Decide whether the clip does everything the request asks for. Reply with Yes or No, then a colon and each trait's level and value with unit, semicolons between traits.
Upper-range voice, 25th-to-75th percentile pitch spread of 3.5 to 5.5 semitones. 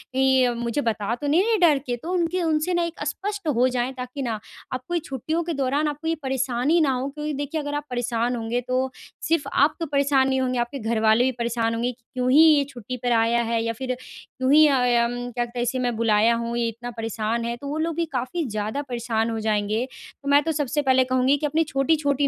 Yes: very high, 255 Hz; average, 3.8 semitones